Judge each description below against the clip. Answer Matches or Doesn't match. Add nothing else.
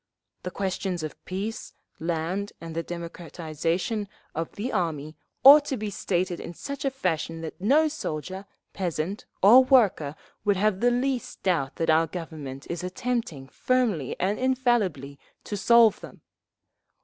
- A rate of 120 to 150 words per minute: Matches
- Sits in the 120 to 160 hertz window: Doesn't match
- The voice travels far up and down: Matches